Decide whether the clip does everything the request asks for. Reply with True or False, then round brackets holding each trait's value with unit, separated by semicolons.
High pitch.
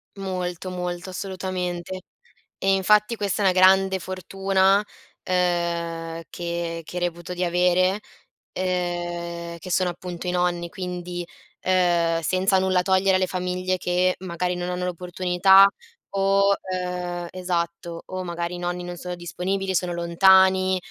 False (180 Hz)